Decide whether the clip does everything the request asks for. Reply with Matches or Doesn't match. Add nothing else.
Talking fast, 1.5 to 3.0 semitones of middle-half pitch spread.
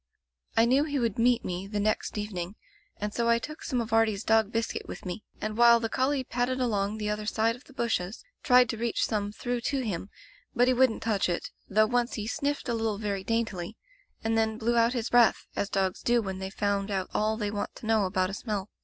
Matches